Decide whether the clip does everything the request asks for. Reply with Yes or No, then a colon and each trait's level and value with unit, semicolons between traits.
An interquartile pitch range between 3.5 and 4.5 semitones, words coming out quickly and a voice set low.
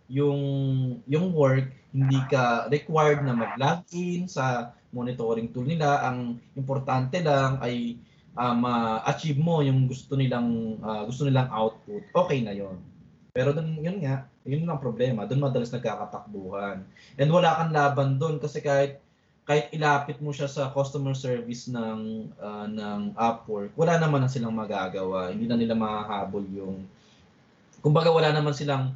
No: average, 4.1 semitones; average, 145 wpm; low, 130 Hz